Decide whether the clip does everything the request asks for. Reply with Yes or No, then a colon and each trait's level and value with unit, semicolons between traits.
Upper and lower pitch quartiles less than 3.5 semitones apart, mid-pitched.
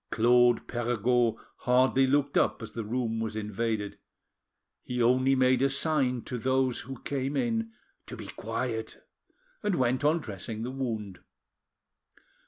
No: average, 2.8 semitones; low, 125 Hz